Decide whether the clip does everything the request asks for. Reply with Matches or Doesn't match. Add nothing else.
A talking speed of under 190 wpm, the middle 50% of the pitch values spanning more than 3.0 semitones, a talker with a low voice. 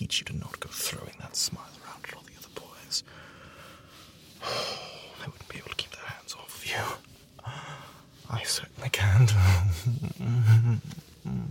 Matches